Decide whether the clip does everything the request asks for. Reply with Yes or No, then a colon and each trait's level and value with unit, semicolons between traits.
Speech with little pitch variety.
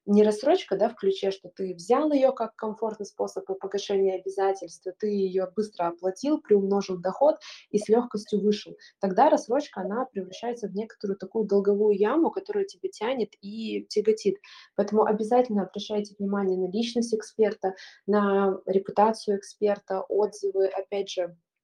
Yes: narrow, 2.1 semitones